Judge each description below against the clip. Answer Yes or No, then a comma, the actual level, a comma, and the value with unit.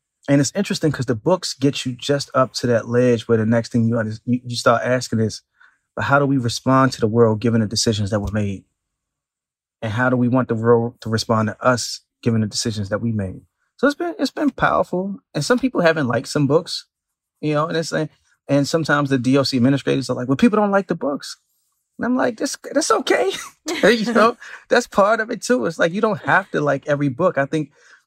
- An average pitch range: No, wide, 6.1 semitones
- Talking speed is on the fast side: Yes, fast, 230 wpm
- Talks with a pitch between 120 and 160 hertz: Yes, low, 135 Hz